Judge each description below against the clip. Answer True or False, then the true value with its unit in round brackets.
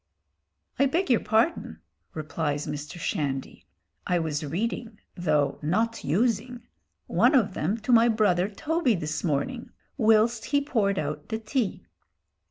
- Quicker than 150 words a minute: False (135 wpm)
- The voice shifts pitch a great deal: True (7.2 semitones)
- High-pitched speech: True (210 Hz)